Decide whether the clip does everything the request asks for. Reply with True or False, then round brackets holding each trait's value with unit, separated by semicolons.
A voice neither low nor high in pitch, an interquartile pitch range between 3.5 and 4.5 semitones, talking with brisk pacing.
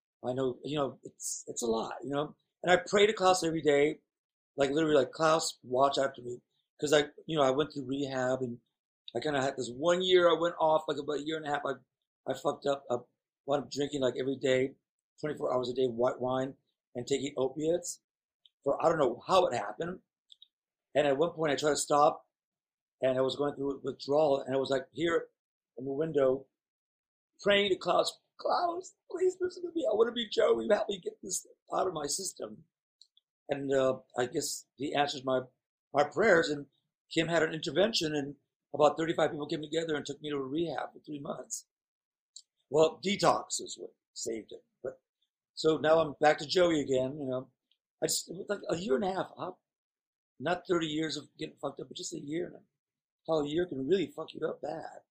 True (150 Hz; 3.8 semitones; 215 wpm)